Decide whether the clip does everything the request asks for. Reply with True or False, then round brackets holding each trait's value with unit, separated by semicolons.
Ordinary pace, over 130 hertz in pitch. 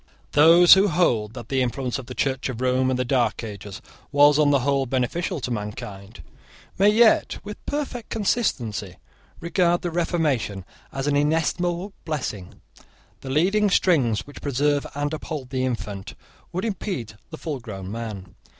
True (155 wpm; 140 Hz)